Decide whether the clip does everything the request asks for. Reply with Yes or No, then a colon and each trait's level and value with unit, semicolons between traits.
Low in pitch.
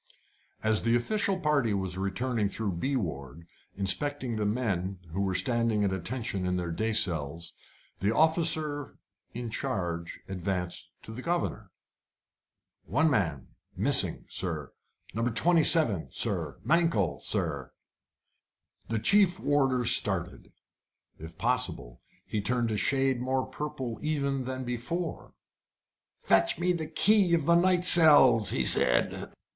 Yes: low, 115 Hz